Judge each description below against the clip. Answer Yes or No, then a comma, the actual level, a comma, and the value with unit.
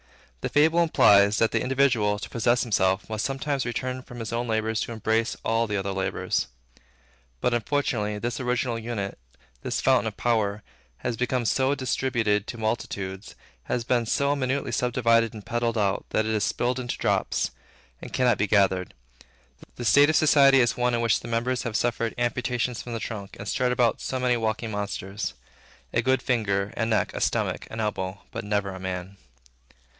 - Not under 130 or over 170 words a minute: No, average, 180 wpm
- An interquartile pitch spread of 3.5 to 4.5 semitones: No, average, 3.0 semitones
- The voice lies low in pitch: Yes, low, 115 Hz